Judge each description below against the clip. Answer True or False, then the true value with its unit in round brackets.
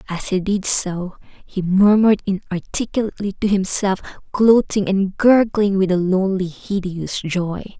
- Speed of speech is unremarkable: False (130 wpm)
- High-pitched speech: True (195 Hz)